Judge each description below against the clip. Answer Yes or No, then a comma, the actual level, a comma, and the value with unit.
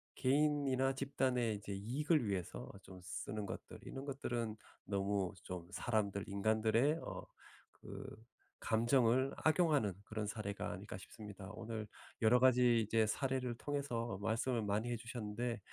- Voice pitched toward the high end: No, low, 115 Hz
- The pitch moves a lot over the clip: No, average, 4.1 semitones